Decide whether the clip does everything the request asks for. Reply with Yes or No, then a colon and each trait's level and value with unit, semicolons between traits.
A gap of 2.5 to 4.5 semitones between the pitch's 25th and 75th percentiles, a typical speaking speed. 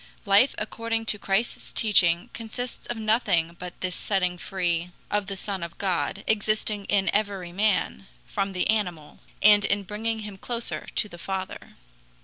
Yes: average, 2.8 semitones; average, 155 wpm